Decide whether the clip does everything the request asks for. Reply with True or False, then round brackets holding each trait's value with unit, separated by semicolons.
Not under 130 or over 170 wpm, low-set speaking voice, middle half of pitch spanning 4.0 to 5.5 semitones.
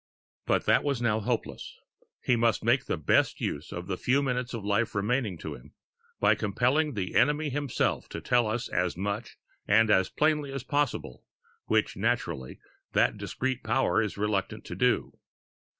True (165 wpm; 115 Hz; 4.8 semitones)